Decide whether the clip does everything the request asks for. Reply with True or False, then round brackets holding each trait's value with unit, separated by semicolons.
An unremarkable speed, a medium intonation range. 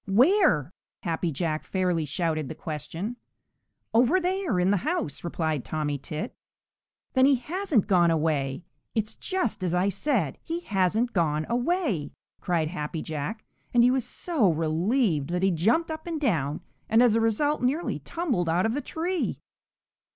False (160 wpm; 8.4 semitones)